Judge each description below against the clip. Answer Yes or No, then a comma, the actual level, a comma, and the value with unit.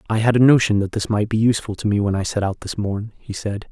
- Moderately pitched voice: No, low, 105 Hz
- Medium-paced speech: No, fast, 305 wpm